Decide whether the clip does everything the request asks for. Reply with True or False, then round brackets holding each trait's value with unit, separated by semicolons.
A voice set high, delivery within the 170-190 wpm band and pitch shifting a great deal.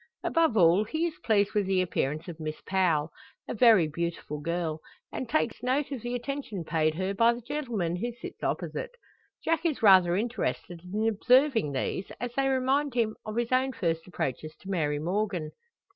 True (210 Hz; 180 wpm; 6.7 semitones)